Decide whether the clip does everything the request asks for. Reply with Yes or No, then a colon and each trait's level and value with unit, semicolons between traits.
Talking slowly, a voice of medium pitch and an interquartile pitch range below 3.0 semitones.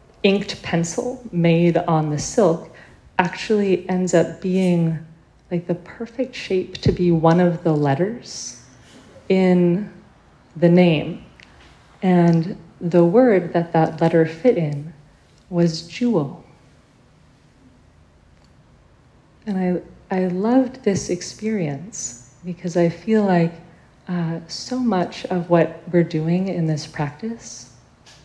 Yes: slow, 115 wpm; medium, 170 Hz; narrow, 2.6 semitones